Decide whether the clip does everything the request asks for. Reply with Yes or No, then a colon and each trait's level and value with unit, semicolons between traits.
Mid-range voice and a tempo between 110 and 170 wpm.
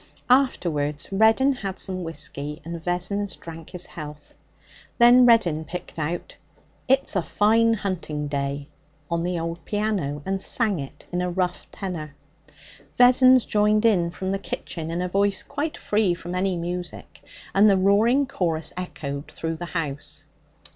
Yes: medium, 180 Hz; average, 150 wpm